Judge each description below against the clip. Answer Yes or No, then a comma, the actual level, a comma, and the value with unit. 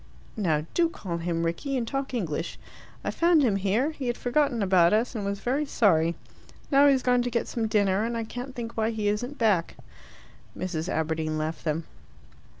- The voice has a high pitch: Yes, high, 220 Hz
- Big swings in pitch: Yes, wide, 6.5 semitones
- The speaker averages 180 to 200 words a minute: Yes, average, 190 wpm